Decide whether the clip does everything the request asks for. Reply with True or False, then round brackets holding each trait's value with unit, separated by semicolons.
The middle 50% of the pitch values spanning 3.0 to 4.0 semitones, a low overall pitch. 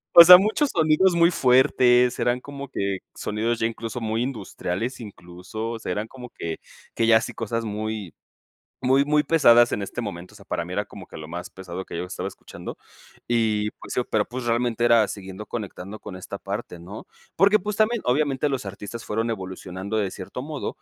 False (4.6 semitones; 115 Hz)